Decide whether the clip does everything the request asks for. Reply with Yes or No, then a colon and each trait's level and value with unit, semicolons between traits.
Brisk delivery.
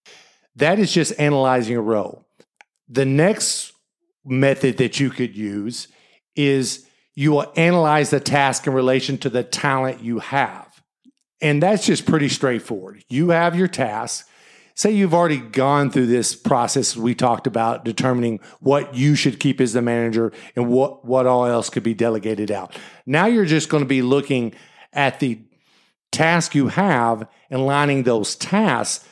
No: average, 160 wpm